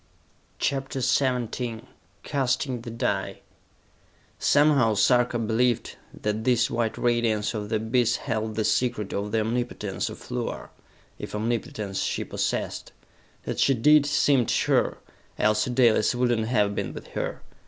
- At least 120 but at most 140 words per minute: Yes, slow, 135 wpm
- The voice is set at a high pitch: No, low, 115 Hz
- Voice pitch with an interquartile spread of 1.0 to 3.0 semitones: Yes, narrow, 2.5 semitones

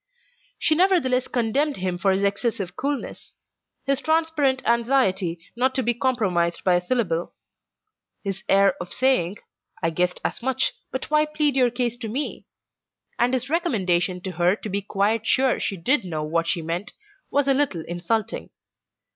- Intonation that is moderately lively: No, wide, 6.4 semitones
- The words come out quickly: No, average, 165 wpm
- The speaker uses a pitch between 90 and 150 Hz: No, high, 225 Hz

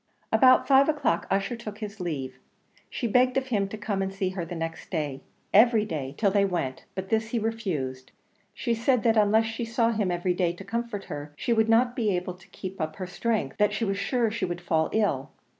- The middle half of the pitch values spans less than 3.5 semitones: No, average, 4.5 semitones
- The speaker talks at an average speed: No, fast, 225 wpm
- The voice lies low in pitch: No, high, 200 Hz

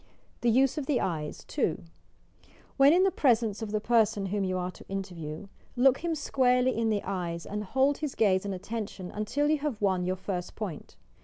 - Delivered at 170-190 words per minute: No, average, 200 wpm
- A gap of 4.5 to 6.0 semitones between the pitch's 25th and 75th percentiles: Yes, wide, 5.6 semitones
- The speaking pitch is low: No, high, 210 Hz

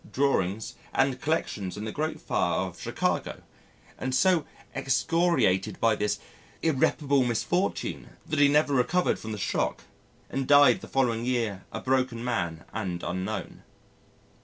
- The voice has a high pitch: No, low, 130 Hz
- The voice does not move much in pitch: No, average, 5.0 semitones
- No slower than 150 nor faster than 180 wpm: No, average, 140 wpm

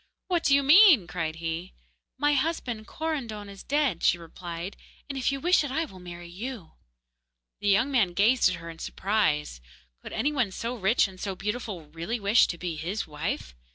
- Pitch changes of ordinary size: No, wide, 7.3 semitones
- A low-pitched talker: No, high, 205 Hz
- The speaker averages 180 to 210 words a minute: Yes, average, 190 wpm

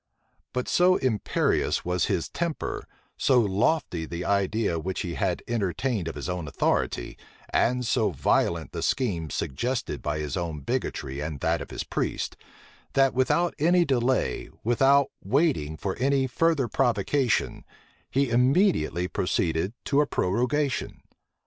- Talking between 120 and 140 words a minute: Yes, slow, 135 wpm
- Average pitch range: No, wide, 7.7 semitones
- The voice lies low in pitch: Yes, low, 115 Hz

